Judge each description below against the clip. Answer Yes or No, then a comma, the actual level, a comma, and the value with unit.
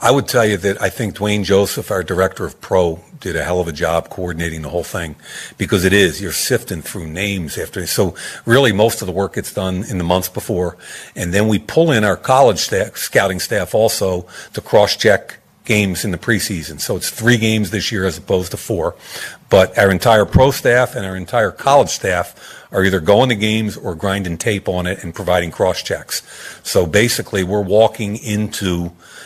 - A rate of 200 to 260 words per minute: Yes, fast, 205 wpm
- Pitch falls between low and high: No, low, 100 Hz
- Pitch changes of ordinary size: Yes, average, 3.0 semitones